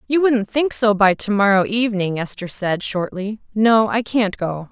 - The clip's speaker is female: Yes, female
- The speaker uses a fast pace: No, average, 190 wpm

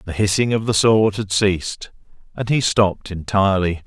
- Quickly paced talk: No, average, 170 wpm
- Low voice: Yes, low, 100 Hz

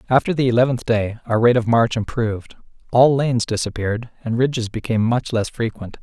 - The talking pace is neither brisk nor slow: Yes, average, 180 wpm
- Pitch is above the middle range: No, low, 115 Hz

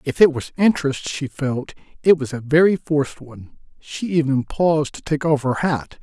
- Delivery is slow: No, average, 200 wpm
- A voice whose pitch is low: No, medium, 145 Hz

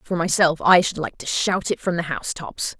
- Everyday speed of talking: No, fast, 260 wpm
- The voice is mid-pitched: Yes, medium, 170 Hz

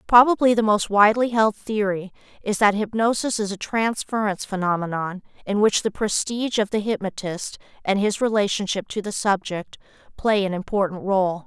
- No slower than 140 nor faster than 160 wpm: Yes, average, 155 wpm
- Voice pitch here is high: Yes, high, 205 Hz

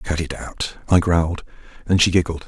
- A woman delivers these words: No, male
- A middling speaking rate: Yes, average, 195 wpm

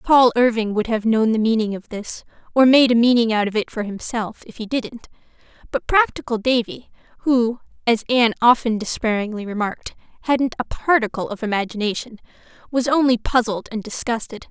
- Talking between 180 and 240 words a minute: No, average, 165 wpm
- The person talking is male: No, female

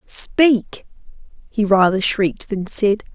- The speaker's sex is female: Yes, female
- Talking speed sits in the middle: No, slow, 115 wpm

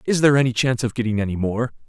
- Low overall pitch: Yes, low, 120 Hz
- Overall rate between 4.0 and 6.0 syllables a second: No, 7.9 syllables/s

